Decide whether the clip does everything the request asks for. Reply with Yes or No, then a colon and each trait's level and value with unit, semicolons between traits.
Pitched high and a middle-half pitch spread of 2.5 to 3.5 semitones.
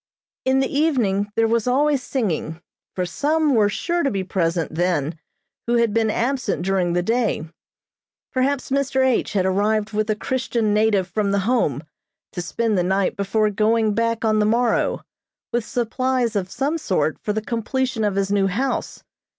No: high, 220 Hz; average, 4.5 semitones